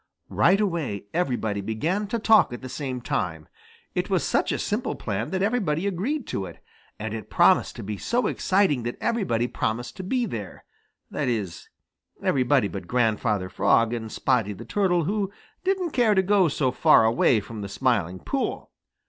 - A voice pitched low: Yes, low, 130 Hz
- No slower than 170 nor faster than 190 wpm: Yes, average, 175 wpm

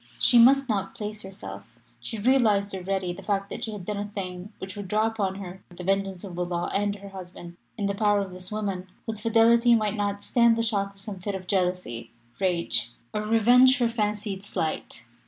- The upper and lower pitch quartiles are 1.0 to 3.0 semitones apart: Yes, narrow, 2.6 semitones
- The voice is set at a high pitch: Yes, high, 200 Hz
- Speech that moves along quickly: Yes, fast, 210 wpm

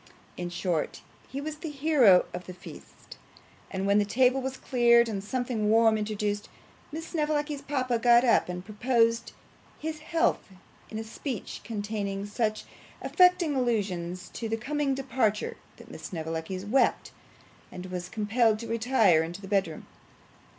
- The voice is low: No, high, 225 Hz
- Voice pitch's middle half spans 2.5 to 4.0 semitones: No, average, 5.0 semitones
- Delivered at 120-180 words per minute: Yes, average, 150 wpm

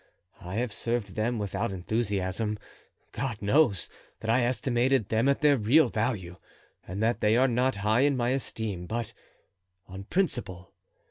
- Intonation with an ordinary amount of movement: Yes, average, 3.7 semitones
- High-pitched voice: No, low, 115 Hz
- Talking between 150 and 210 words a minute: No, average, 140 wpm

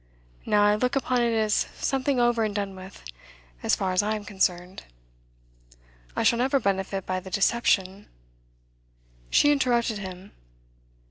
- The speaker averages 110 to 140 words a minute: No, average, 150 wpm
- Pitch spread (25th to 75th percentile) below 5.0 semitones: Yes, average, 4.2 semitones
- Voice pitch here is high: Yes, high, 205 Hz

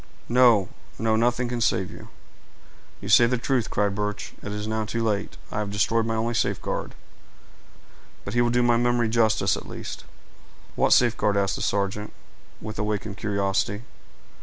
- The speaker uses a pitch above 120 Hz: No, low, 110 Hz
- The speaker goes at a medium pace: Yes, average, 160 wpm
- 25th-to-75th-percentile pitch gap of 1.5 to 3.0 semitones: Yes, narrow, 2.4 semitones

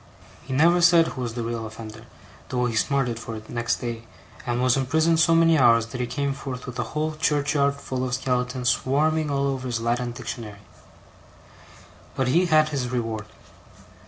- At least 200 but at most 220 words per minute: No, average, 185 wpm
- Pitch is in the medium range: No, low, 125 Hz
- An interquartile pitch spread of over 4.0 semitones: No, average, 3.6 semitones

